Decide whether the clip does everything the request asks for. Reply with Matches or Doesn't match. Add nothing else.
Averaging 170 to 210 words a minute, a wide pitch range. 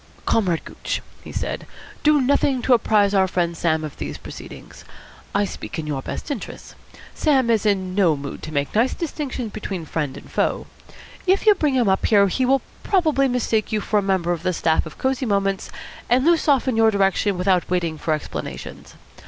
Matches